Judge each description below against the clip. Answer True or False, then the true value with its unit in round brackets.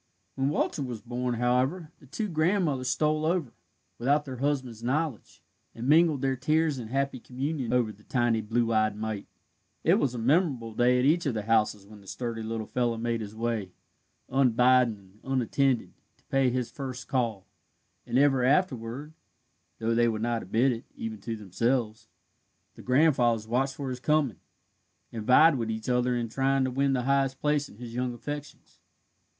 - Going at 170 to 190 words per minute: True (180 wpm)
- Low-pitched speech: True (125 Hz)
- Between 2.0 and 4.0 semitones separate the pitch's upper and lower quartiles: True (3.3 semitones)